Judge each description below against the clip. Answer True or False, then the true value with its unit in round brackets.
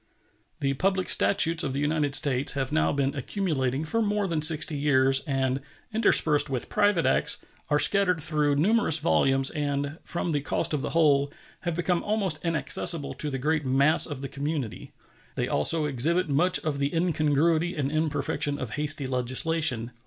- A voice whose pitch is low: False (150 Hz)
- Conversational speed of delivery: True (165 wpm)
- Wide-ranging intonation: False (3.2 semitones)